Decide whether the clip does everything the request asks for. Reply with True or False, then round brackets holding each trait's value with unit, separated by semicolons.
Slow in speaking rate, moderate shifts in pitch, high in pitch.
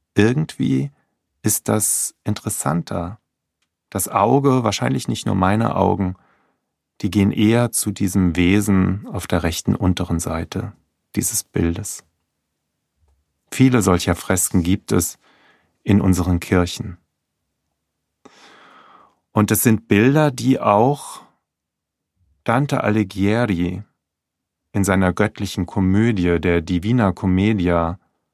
False (100 wpm; 3.7 semitones; 95 Hz)